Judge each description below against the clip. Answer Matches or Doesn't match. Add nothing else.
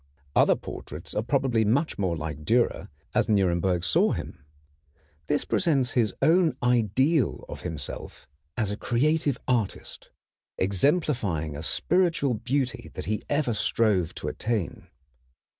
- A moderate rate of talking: Doesn't match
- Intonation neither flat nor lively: Doesn't match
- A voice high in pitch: Doesn't match